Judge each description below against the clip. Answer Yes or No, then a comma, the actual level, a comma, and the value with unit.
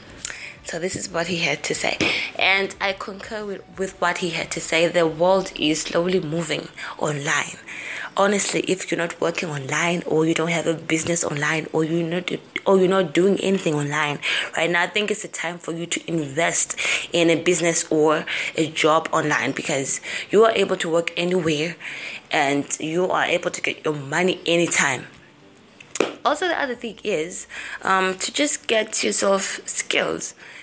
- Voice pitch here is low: No, medium, 170 Hz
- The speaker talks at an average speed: Yes, average, 180 wpm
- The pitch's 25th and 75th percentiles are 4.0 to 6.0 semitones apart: No, average, 2.8 semitones